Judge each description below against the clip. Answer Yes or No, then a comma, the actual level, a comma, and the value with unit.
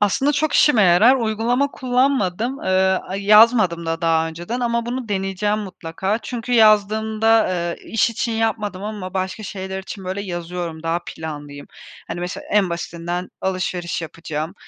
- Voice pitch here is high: Yes, high, 195 Hz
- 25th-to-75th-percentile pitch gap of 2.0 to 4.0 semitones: No, average, 4.5 semitones